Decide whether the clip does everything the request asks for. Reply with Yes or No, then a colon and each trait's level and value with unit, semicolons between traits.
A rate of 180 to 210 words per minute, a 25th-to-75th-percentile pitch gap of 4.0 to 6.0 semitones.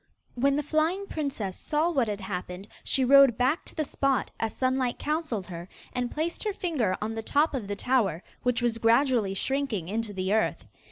Yes: average, 190 wpm; average, 5.3 semitones